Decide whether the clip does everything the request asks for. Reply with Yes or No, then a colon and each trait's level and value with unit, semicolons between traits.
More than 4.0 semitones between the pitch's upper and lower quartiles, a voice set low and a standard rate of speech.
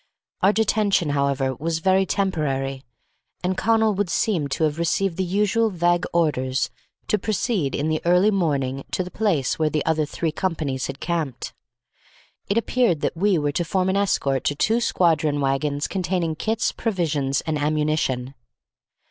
No: average, 5.0 semitones; medium, 165 Hz; average, 160 wpm